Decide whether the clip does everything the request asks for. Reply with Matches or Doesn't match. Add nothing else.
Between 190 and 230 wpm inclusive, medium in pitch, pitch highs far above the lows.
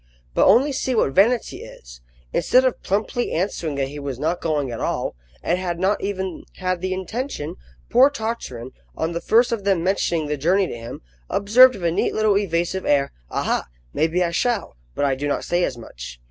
Matches